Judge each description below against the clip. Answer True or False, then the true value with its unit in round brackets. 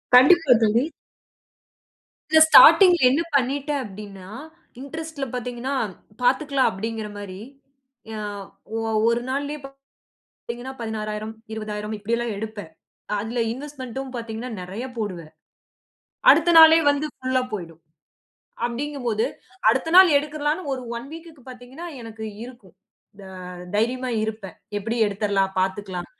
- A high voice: True (240 Hz)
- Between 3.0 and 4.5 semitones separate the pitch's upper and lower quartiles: False (4.9 semitones)